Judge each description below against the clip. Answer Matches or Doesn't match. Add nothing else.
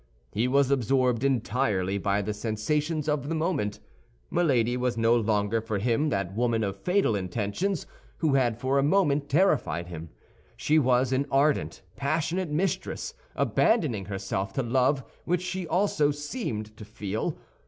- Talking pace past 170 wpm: Doesn't match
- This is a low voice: Matches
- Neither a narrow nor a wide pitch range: Doesn't match